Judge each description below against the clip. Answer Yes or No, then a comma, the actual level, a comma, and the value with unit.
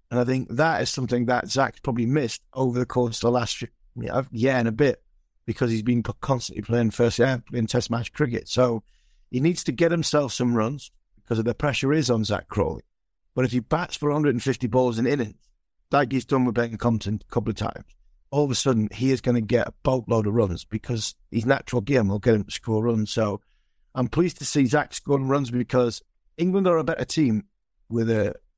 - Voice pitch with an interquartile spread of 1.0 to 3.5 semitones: Yes, average, 3.0 semitones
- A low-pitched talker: Yes, low, 125 Hz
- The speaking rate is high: Yes, fast, 225 wpm